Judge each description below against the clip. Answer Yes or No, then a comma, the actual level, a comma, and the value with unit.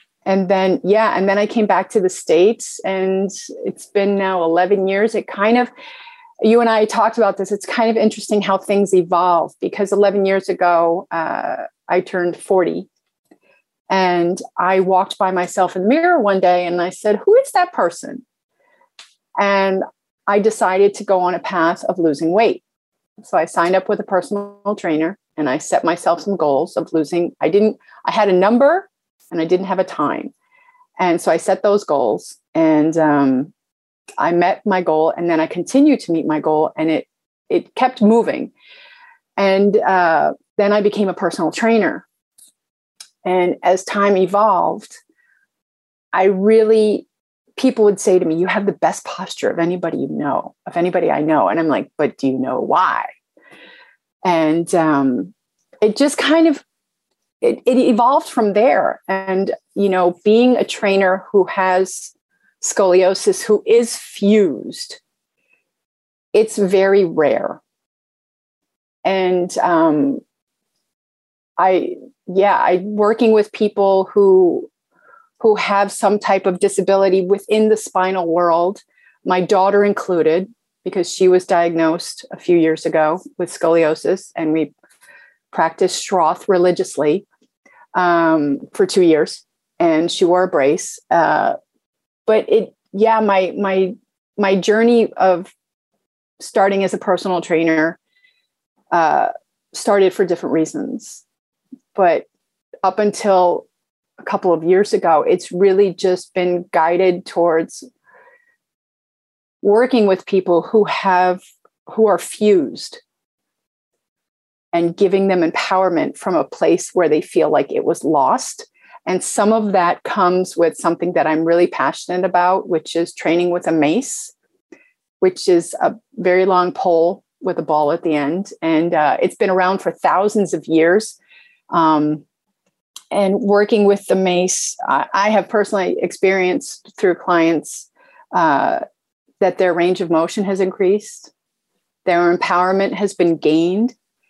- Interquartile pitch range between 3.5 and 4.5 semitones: Yes, average, 4.2 semitones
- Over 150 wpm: No, average, 145 wpm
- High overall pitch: Yes, high, 195 Hz